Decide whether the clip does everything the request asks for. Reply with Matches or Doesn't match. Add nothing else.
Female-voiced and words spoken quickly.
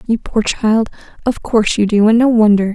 Matches